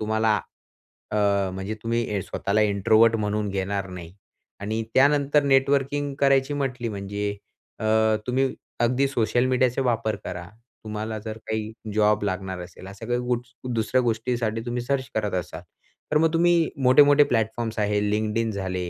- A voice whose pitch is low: Yes, low, 110 Hz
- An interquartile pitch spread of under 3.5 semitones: No, average, 3.9 semitones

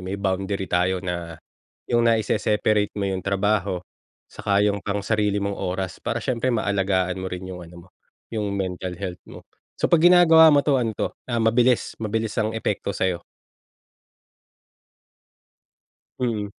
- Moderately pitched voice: No, low, 100 Hz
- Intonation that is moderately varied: Yes, average, 3.1 semitones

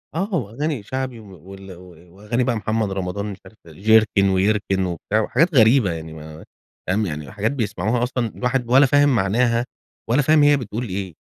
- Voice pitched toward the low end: Yes, low, 110 Hz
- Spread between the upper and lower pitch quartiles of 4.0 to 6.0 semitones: Yes, average, 4.7 semitones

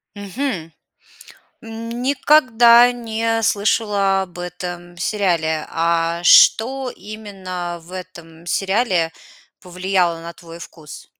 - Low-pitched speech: No, high, 190 Hz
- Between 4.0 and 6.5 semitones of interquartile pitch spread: Yes, average, 4.7 semitones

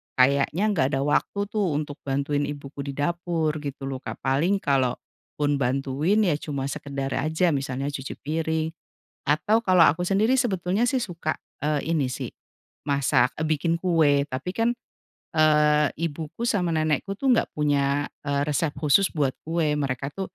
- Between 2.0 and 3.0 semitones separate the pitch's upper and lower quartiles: No, average, 3.6 semitones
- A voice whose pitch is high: No, medium, 150 Hz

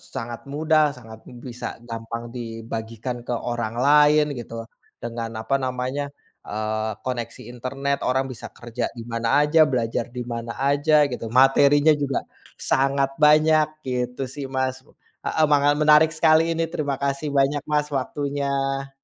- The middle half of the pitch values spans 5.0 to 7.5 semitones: No, average, 3.7 semitones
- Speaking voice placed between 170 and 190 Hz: No, low, 135 Hz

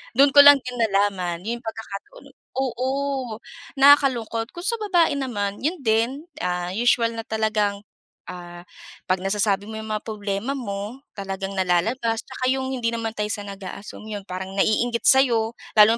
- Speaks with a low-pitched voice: No, high, 220 Hz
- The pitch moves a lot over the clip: No, average, 4.1 semitones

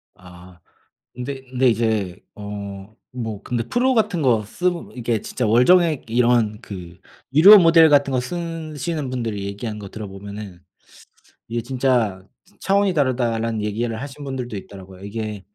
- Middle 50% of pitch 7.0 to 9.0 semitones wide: No, average, 5.3 semitones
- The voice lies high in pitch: No, low, 120 Hz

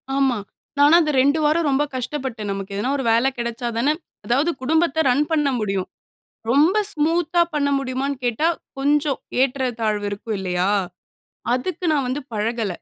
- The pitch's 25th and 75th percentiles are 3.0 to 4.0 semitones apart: No, average, 4.5 semitones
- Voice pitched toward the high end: Yes, very high, 265 Hz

